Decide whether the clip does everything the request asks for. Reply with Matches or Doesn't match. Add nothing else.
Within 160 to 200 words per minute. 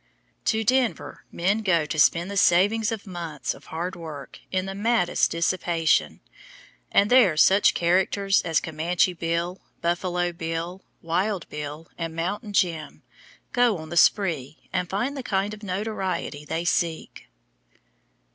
Doesn't match